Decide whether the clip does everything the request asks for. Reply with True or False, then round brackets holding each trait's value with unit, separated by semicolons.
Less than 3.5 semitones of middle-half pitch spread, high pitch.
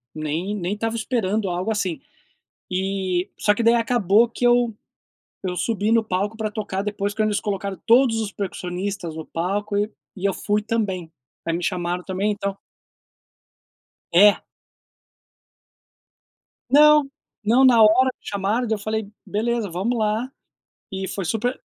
True (3.0 semitones; 205 Hz)